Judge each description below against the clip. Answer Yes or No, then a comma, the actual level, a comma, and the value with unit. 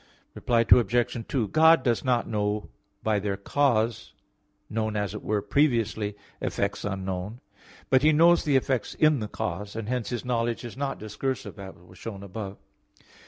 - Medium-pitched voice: No, low, 115 Hz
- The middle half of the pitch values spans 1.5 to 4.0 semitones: Yes, average, 3.7 semitones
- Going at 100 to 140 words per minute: No, average, 165 wpm